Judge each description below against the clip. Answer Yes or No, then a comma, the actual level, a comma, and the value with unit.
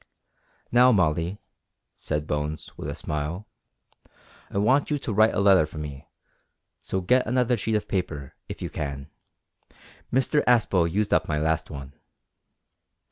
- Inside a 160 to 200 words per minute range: No, average, 145 wpm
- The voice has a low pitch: Yes, very low, 90 Hz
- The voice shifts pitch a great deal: Yes, wide, 6.7 semitones